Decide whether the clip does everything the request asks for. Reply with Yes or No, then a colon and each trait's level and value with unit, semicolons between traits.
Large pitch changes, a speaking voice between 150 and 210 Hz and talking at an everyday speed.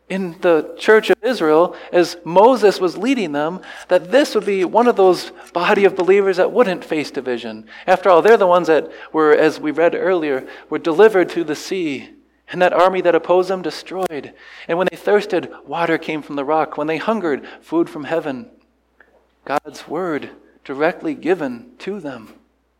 Yes: wide, 5.8 semitones; medium, 185 Hz; average, 180 wpm